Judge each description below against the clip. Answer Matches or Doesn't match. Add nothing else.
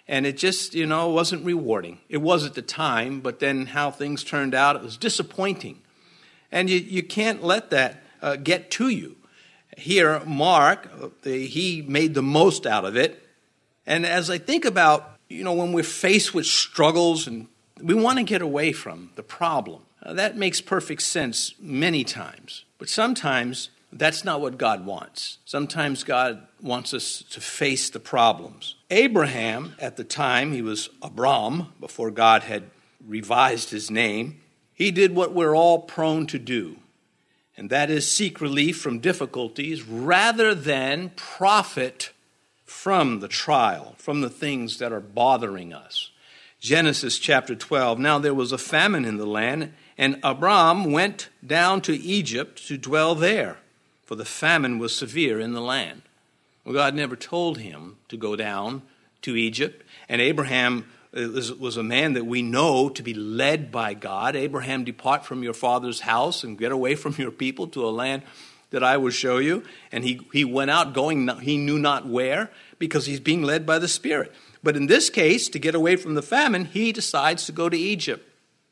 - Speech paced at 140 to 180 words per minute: Matches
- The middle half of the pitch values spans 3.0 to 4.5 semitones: Doesn't match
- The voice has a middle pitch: Matches